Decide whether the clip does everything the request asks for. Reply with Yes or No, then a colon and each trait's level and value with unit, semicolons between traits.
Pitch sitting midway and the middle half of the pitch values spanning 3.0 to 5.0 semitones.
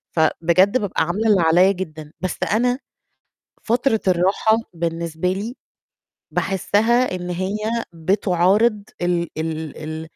Yes: medium, 180 Hz; average, 3.9 semitones